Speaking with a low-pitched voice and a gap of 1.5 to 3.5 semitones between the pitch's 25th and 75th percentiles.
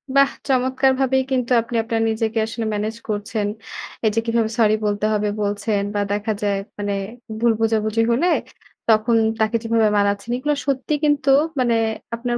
No: high, 225 Hz; average, 2.8 semitones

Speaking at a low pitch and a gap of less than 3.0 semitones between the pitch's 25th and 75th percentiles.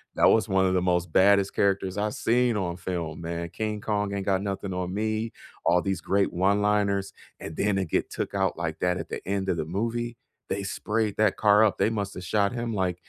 Yes: low, 100 Hz; narrow, 2.4 semitones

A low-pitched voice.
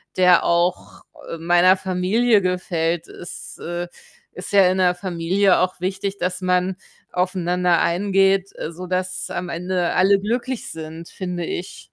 No: medium, 180 Hz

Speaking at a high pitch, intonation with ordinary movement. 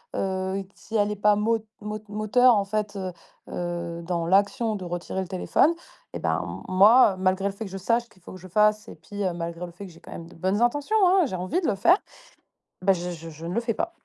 Yes: high, 195 Hz; average, 3.1 semitones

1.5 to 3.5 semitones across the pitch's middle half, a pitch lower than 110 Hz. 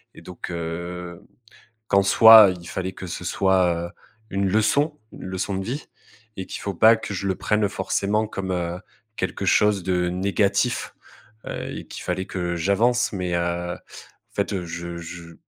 Yes: narrow, 2.4 semitones; very low, 95 Hz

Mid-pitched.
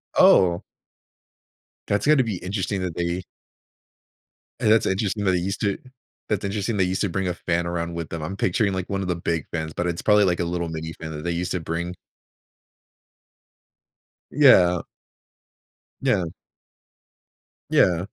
No: very low, 90 Hz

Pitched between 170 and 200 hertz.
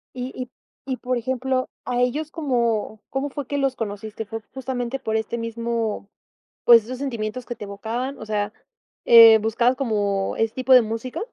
No: high, 235 Hz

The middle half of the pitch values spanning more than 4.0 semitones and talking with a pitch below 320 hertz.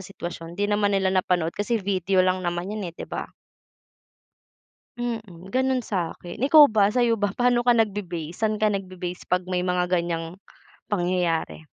No: average, 3.3 semitones; high, 190 Hz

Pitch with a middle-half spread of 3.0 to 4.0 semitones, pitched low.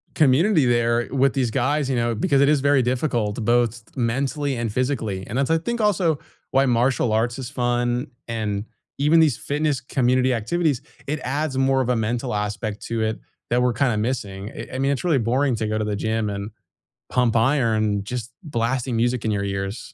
Yes: average, 3.4 semitones; low, 125 Hz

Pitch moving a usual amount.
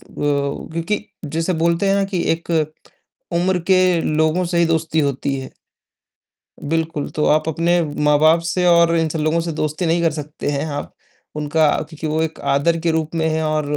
No: narrow, 1.9 semitones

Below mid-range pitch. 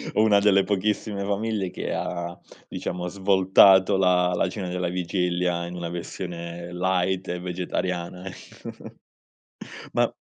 Yes: very low, 90 Hz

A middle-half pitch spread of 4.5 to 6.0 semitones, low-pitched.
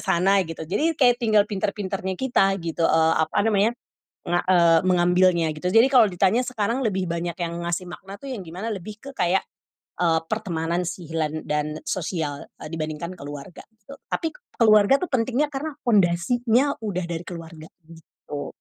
No: average, 5.0 semitones; medium, 185 Hz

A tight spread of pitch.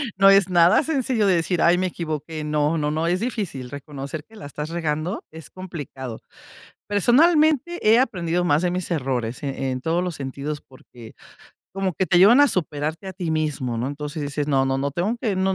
No: average, 4.8 semitones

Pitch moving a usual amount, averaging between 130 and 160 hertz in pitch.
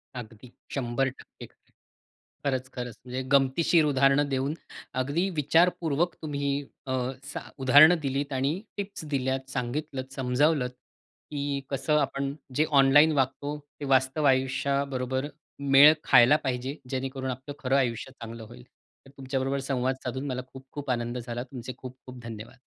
No: narrow, 2.0 semitones; low, 135 Hz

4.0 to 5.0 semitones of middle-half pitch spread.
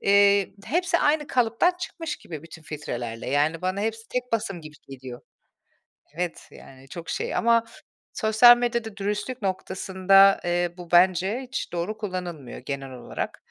No: wide, 5.6 semitones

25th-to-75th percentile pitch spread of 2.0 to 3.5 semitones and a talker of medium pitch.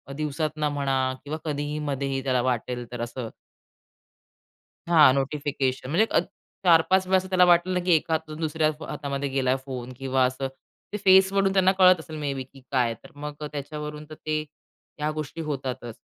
Yes: average, 3.2 semitones; medium, 150 Hz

